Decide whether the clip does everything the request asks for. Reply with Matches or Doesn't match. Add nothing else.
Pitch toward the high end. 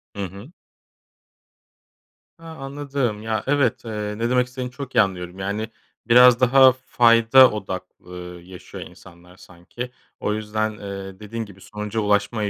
Doesn't match